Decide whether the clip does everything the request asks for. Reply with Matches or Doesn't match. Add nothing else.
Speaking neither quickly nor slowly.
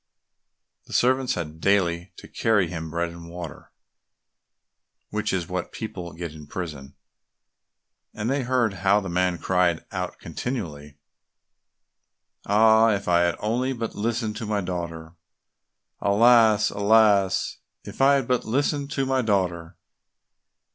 Doesn't match